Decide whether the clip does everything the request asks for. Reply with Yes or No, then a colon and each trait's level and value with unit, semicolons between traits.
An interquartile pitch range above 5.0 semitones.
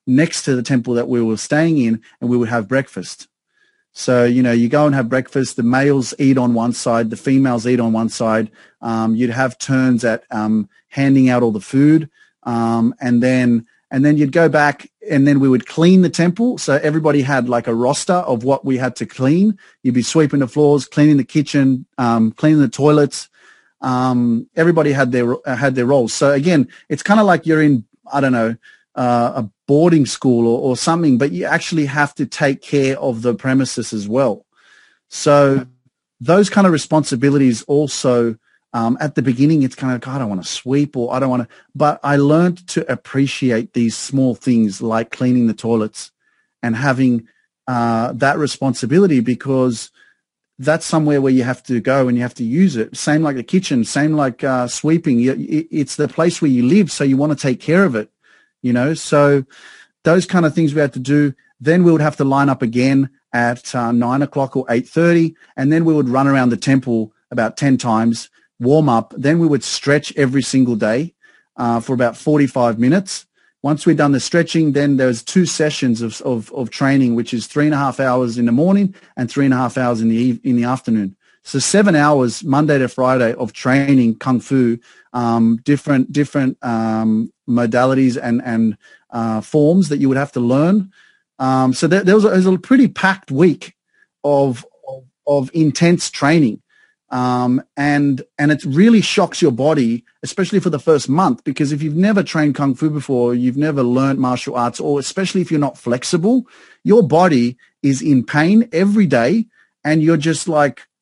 No: average, 3.8 semitones